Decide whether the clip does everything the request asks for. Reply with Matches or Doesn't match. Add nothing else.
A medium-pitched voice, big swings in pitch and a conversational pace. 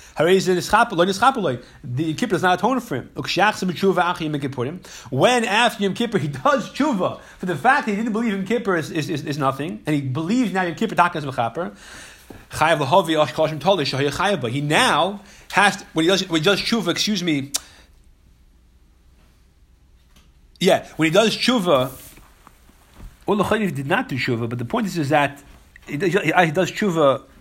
Matches